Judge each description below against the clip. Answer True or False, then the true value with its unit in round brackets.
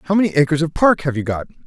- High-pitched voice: False (155 Hz)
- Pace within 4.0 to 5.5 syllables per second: False (7.0 syllables/s)